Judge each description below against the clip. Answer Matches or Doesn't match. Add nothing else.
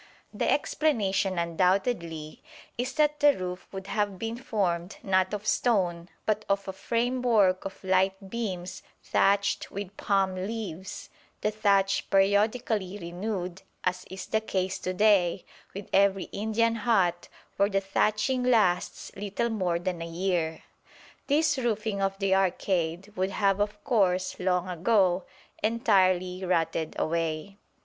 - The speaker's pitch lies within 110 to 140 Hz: Doesn't match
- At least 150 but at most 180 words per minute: Doesn't match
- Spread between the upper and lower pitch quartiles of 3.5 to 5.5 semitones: Doesn't match